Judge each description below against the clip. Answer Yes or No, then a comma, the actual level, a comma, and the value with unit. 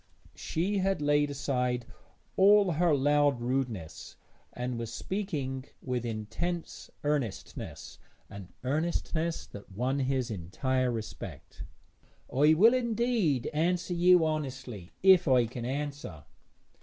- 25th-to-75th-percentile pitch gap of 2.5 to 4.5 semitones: No, wide, 5.6 semitones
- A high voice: No, medium, 140 Hz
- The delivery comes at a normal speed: No, slow, 110 wpm